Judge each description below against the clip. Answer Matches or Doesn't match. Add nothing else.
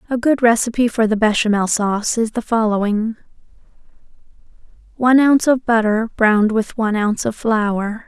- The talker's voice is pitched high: Matches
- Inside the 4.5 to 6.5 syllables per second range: Matches